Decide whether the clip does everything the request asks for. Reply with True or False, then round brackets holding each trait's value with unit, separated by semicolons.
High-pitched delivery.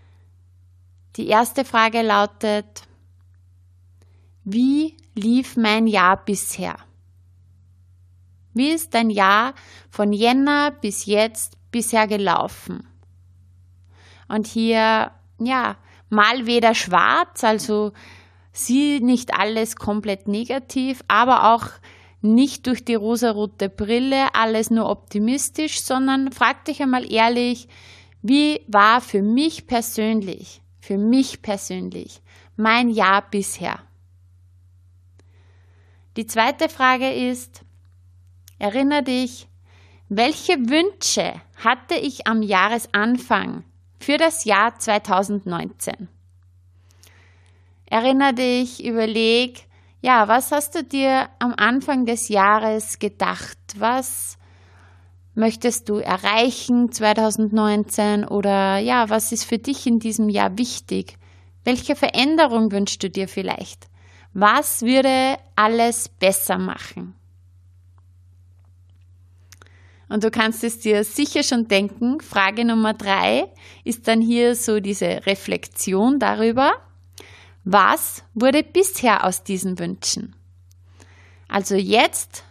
True (210 Hz)